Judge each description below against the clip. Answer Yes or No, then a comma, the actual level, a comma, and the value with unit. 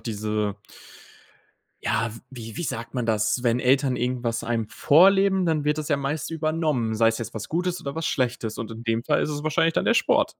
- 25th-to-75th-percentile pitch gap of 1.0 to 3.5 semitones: No, wide, 5.4 semitones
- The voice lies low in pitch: Yes, low, 125 Hz